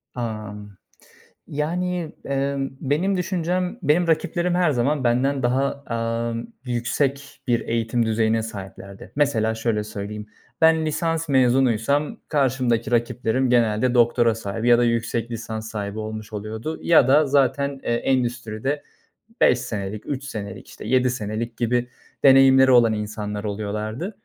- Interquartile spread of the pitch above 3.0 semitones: Yes, average, 4.1 semitones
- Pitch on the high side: No, low, 120 Hz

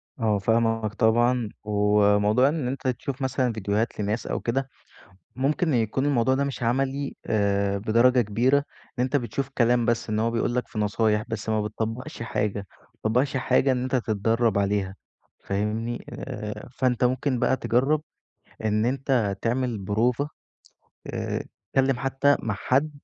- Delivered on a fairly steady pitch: No, average, 3.5 semitones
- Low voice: Yes, low, 115 Hz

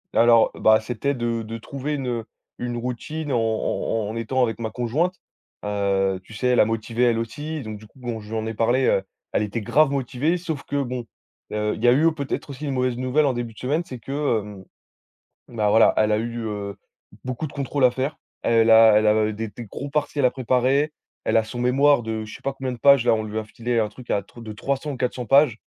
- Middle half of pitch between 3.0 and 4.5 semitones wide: Yes, average, 3.6 semitones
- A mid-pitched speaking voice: No, low, 120 Hz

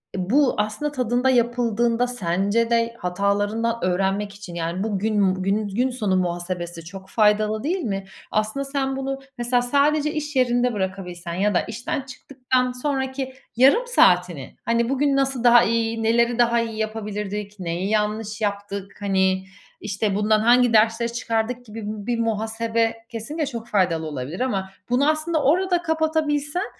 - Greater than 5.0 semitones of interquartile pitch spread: No, average, 4.0 semitones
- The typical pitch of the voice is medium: No, high, 225 Hz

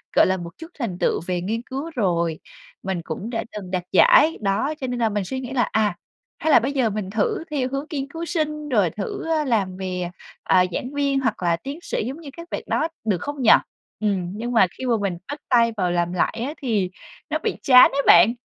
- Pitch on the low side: No, high, 230 Hz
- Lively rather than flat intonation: Yes, wide, 6.6 semitones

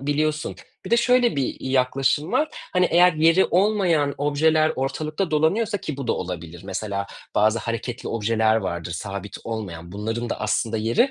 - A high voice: No, low, 135 Hz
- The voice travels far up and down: Yes, wide, 7.0 semitones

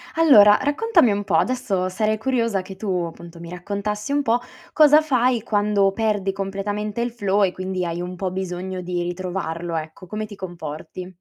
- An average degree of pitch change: Yes, average, 3.4 semitones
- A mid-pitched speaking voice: No, high, 195 Hz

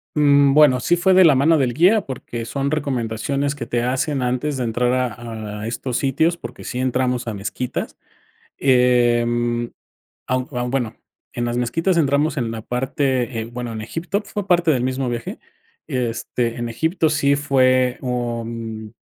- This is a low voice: Yes, low, 125 Hz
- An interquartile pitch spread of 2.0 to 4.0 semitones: Yes, average, 3.1 semitones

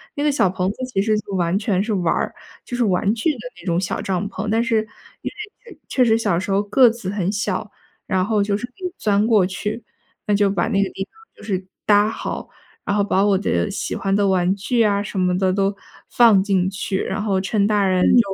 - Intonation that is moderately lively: No, narrow, 2.2 semitones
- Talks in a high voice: Yes, high, 200 Hz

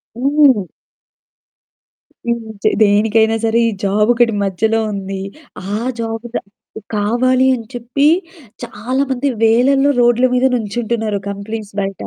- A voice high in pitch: Yes, high, 230 Hz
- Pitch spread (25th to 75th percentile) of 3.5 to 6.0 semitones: No, average, 2.8 semitones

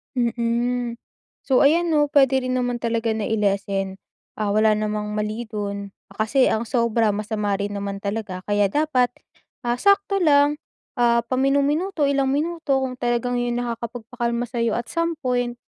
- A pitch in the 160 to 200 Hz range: No, high, 240 Hz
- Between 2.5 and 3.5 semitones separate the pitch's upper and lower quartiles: No, average, 3.9 semitones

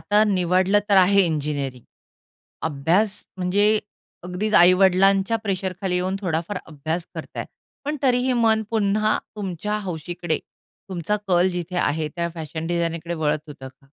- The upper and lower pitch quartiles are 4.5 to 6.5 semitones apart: No, average, 3.7 semitones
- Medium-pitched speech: Yes, medium, 180 Hz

